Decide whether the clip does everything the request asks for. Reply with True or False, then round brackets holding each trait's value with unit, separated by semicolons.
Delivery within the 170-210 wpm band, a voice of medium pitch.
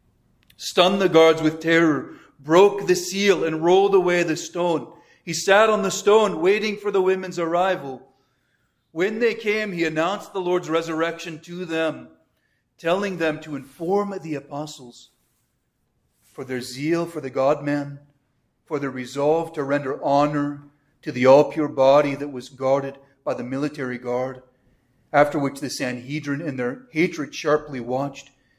False (155 wpm; 150 Hz)